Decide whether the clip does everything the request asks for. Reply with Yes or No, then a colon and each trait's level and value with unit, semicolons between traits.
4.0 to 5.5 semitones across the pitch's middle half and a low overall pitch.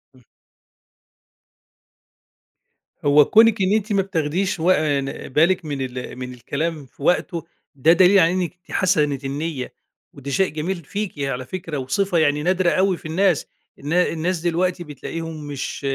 No: average, 4.5 semitones; medium, 165 Hz